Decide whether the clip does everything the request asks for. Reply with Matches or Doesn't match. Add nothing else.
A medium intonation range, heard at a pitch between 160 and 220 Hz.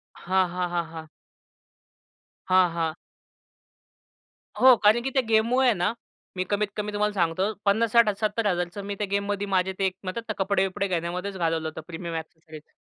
Matches